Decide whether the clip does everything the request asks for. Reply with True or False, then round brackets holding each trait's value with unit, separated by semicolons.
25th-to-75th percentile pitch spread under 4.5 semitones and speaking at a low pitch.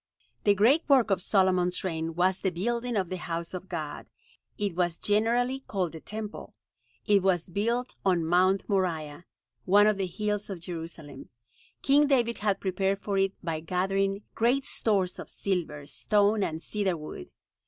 False (3.2 semitones; 190 Hz)